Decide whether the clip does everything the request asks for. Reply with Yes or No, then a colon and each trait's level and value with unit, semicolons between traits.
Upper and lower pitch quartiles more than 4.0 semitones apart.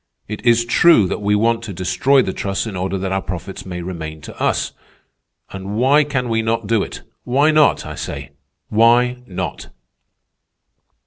Yes: average, 4.4 semitones